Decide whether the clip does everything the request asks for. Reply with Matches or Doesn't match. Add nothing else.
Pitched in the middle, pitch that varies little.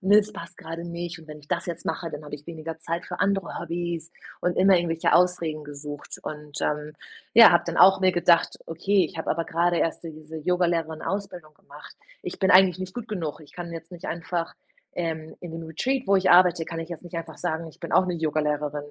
Matches